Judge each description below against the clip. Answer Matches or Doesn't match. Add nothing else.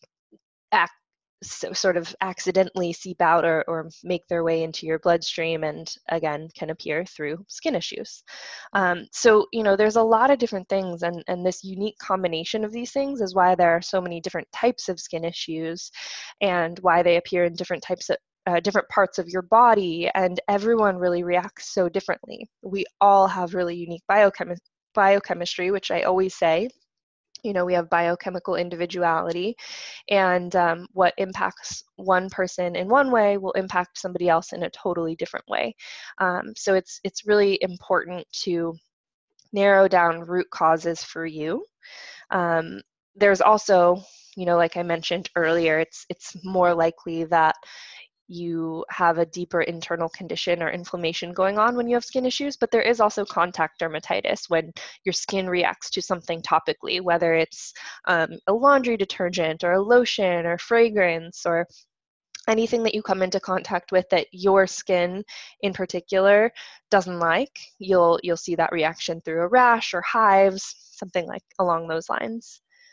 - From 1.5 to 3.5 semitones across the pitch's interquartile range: Matches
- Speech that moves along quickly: Doesn't match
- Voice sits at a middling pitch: Matches